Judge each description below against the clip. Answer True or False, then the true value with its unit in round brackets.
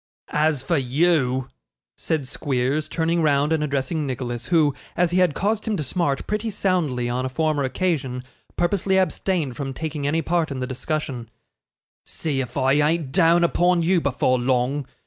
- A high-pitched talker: False (150 Hz)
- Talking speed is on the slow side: False (165 wpm)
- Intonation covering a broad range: False (4.5 semitones)